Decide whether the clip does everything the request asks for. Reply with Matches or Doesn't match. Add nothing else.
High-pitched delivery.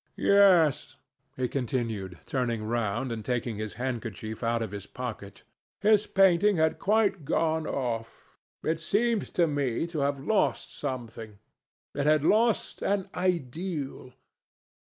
Doesn't match